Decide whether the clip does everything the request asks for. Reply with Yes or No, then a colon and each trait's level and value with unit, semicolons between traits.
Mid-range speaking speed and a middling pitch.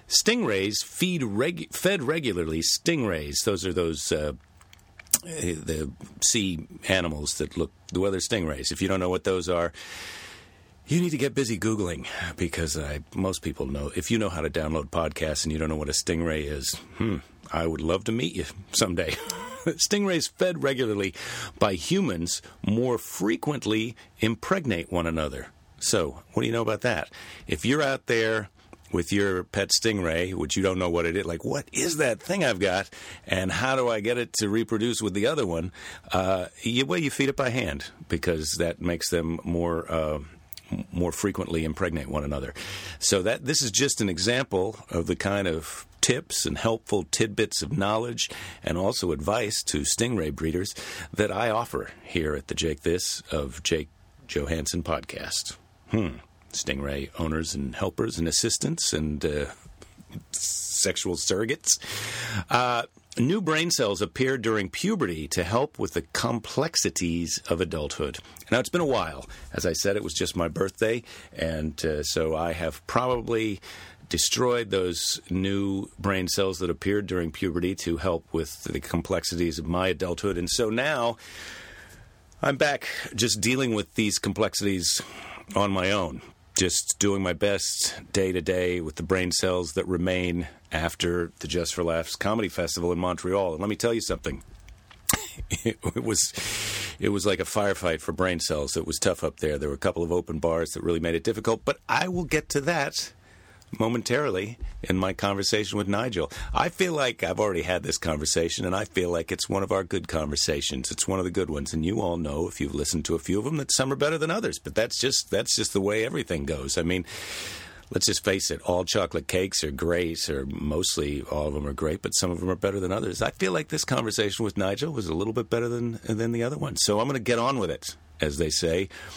No: average, 190 wpm; very low, 90 Hz